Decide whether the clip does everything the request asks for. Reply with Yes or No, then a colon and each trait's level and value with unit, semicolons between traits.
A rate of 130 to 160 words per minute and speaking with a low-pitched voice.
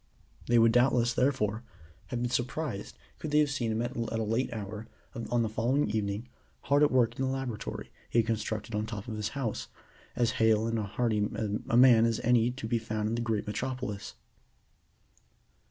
No: average, 190 wpm; low, 115 Hz